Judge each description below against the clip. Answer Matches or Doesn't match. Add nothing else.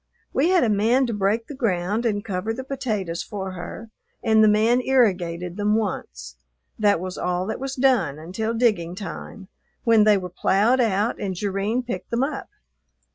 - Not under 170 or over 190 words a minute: Matches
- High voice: Matches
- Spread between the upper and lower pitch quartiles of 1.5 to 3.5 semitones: Doesn't match